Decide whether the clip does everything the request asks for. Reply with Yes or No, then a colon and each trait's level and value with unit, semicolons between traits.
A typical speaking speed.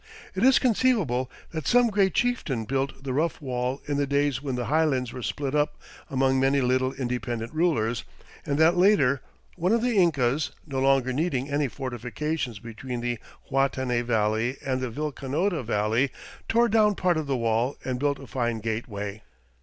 Yes: average, 170 wpm